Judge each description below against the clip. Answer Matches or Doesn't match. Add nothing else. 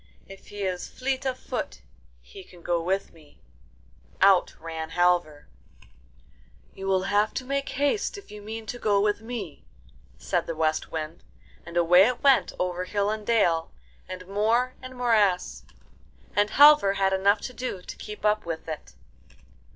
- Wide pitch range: Doesn't match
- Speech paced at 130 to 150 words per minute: Doesn't match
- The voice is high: Matches